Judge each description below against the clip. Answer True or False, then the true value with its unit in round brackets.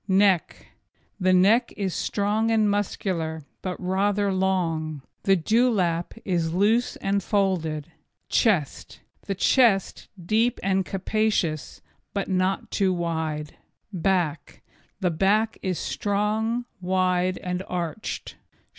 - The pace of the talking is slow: True (110 wpm)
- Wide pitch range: False (2.9 semitones)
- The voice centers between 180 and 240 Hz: True (190 Hz)